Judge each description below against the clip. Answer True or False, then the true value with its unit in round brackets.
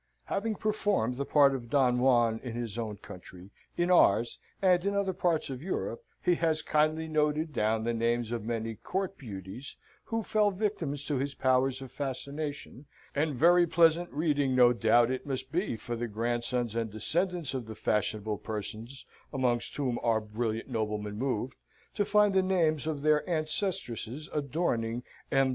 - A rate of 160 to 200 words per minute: True (165 wpm)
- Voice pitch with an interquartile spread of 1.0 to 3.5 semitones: False (5.6 semitones)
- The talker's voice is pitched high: False (135 Hz)